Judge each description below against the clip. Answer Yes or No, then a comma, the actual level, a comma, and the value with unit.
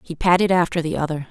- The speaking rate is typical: No, fast, 230 wpm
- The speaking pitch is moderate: Yes, medium, 170 Hz